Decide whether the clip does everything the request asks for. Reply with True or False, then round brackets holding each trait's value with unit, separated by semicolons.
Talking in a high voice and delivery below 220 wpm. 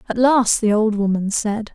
True (220 Hz; 205 wpm)